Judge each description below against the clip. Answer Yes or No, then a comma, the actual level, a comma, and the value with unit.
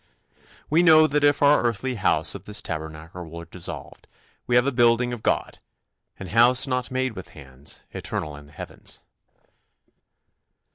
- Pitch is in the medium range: No, low, 115 Hz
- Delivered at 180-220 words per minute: No, average, 155 wpm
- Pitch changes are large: Yes, wide, 7.7 semitones